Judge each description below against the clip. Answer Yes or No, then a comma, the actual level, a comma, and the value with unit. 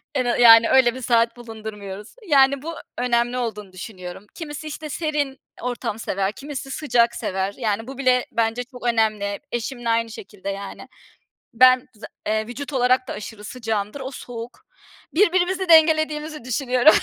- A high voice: Yes, high, 245 Hz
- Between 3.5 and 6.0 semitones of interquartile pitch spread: Yes, average, 3.9 semitones